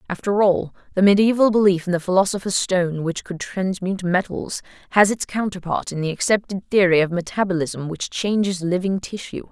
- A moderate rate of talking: Yes, average, 165 wpm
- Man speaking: No, female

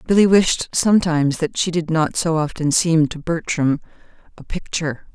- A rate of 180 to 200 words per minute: No, average, 150 wpm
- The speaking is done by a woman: Yes, female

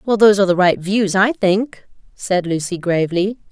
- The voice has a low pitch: No, high, 195 Hz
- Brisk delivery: No, average, 190 wpm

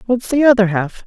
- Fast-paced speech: Yes, fast, 225 wpm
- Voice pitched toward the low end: No, high, 225 Hz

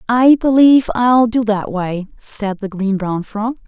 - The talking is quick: No, average, 180 wpm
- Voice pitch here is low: No, high, 220 Hz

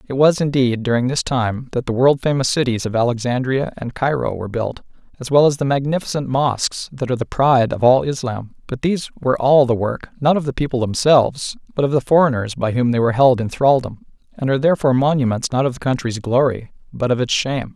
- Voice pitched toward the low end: Yes, low, 130 Hz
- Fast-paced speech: Yes, fast, 220 wpm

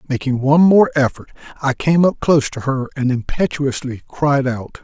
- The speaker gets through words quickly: No, average, 175 wpm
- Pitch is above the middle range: No, medium, 140 Hz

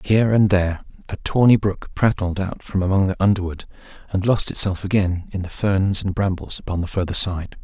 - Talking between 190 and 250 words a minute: Yes, average, 195 wpm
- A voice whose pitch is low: Yes, very low, 95 Hz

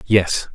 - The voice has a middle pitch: No, low, 100 Hz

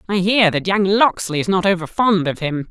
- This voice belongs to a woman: No, male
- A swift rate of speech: Yes, fast, 245 wpm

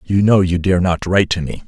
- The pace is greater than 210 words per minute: Yes, fast, 285 wpm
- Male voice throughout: Yes, male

